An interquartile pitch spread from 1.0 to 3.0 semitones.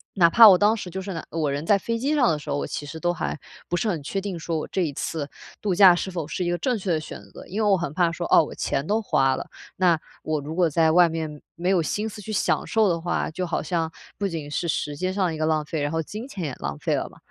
No: average, 3.7 semitones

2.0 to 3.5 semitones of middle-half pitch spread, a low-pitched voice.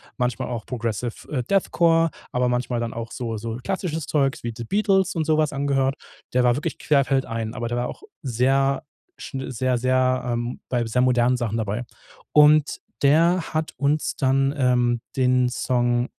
Yes: average, 2.9 semitones; low, 125 Hz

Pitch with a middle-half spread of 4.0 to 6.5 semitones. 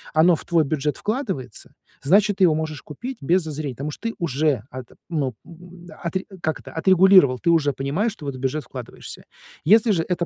Yes: average, 4.6 semitones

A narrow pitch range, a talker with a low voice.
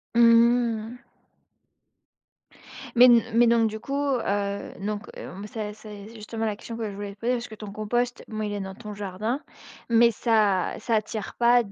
No: narrow, 2.3 semitones; high, 220 Hz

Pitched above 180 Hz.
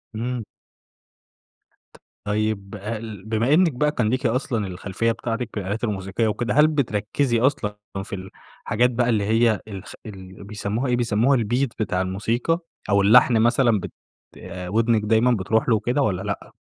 No: low, 110 Hz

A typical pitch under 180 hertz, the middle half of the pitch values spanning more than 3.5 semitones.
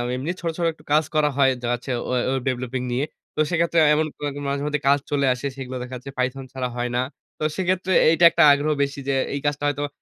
No: medium, 140 Hz; average, 2.8 semitones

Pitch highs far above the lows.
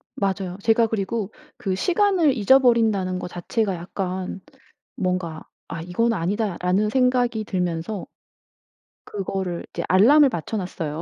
No: average, 4.1 semitones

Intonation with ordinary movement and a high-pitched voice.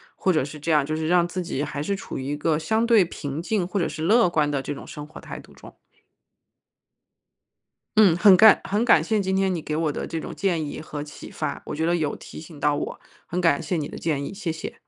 No: average, 4.0 semitones; medium, 165 Hz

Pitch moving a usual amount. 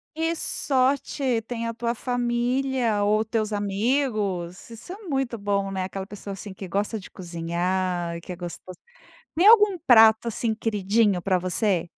Yes: average, 4.4 semitones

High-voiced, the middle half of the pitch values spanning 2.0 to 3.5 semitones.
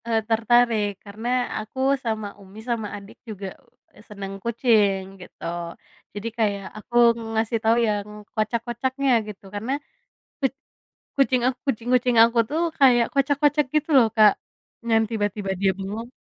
Yes: high, 225 Hz; average, 2.9 semitones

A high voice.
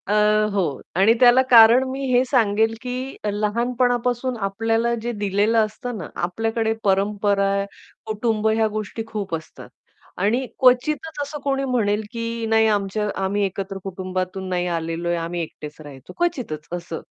Yes: high, 215 Hz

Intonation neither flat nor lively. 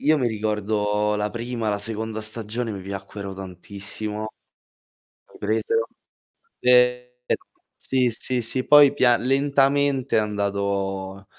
Yes: average, 3.5 semitones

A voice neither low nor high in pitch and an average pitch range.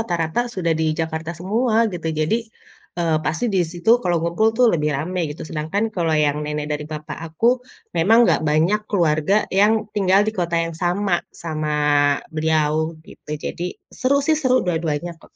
Yes: medium, 170 Hz; average, 3.9 semitones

